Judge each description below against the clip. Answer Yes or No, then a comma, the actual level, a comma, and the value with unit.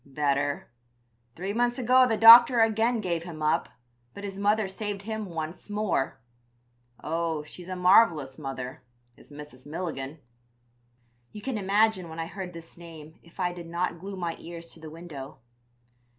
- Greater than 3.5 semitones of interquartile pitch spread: Yes, average, 4.8 semitones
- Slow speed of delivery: No, average, 160 wpm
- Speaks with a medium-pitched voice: Yes, medium, 175 Hz